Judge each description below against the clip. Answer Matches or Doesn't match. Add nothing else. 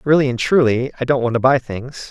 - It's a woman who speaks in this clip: Doesn't match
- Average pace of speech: Doesn't match